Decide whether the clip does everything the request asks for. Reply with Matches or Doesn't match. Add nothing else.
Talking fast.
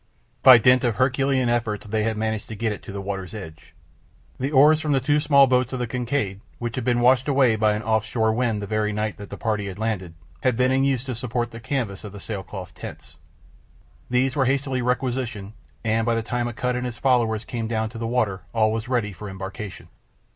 Matches